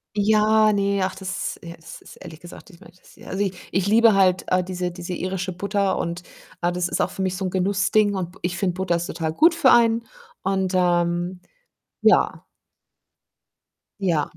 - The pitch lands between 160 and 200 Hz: Yes, medium, 185 Hz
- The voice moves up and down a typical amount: No, narrow, 2.2 semitones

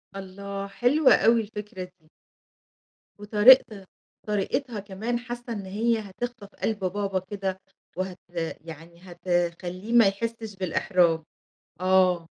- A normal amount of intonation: Yes, average, 3.3 semitones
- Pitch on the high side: Yes, high, 200 Hz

